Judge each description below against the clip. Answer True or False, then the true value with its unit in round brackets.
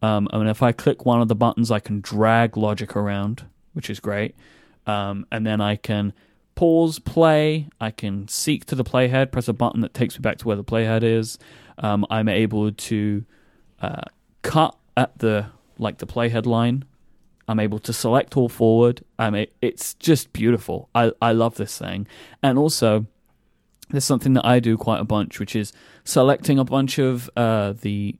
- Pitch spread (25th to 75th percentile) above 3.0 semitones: False (2.5 semitones)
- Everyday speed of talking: True (190 wpm)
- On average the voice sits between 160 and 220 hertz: False (115 Hz)